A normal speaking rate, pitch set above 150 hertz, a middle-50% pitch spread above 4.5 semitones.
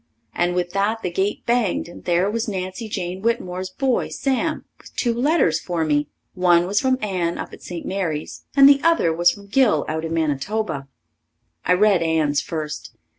Yes: average, 180 wpm; medium, 185 Hz; average, 5.0 semitones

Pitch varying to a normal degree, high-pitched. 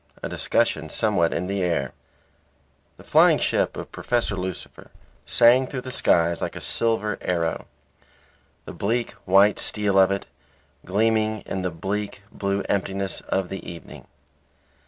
No: average, 3.0 semitones; low, 100 Hz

